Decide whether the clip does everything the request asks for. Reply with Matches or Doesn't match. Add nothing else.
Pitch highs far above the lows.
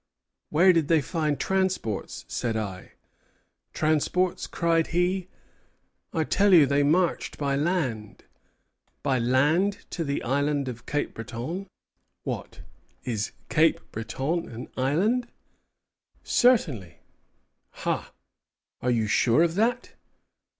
Matches